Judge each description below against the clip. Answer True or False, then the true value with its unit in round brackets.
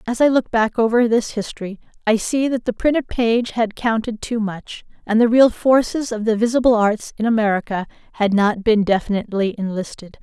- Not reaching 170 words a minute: False (190 wpm)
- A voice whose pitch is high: True (225 Hz)